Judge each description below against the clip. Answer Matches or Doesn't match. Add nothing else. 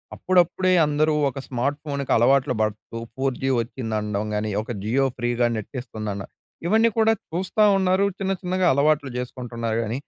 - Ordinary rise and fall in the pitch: Doesn't match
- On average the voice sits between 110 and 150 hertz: Matches